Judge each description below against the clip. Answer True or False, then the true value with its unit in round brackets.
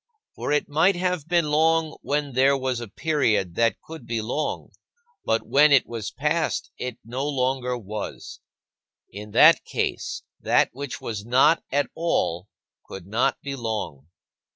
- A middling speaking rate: True (155 wpm)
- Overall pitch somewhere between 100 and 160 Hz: True (135 Hz)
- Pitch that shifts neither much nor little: True (4.9 semitones)